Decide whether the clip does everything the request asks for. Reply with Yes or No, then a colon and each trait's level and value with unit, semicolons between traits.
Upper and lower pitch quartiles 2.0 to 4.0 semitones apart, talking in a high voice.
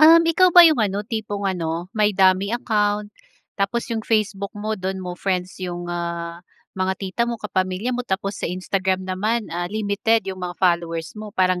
Yes: average, 2.7 semitones; high, 195 Hz